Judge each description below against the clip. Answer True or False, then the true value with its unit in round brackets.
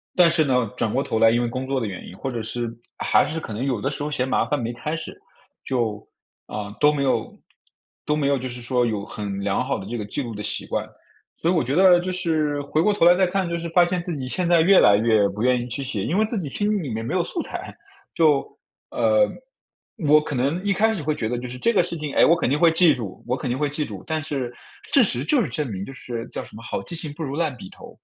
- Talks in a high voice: False (140 Hz)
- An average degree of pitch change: False (5.8 semitones)